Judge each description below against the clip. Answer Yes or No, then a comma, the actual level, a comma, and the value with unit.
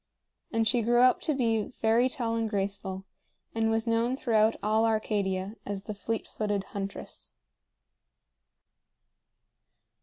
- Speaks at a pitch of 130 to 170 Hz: No, high, 220 Hz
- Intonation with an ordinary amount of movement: No, narrow, 2.1 semitones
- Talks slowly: Yes, slow, 125 wpm